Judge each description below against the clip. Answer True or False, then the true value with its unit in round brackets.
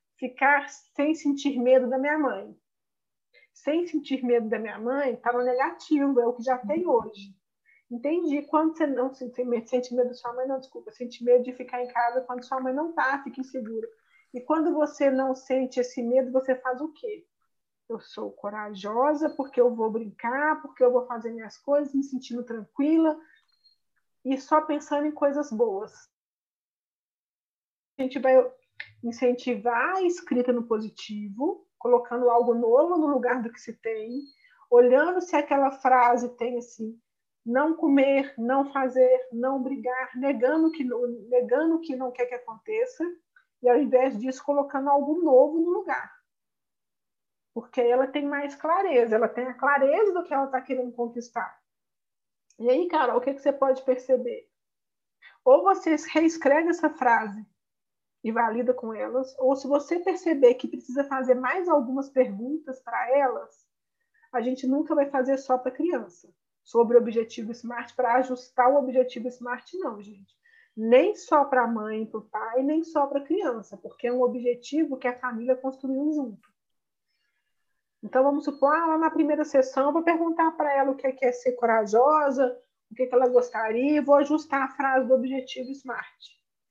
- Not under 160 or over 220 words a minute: True (170 wpm)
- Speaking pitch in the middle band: False (260 Hz)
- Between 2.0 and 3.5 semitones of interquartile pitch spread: True (3.2 semitones)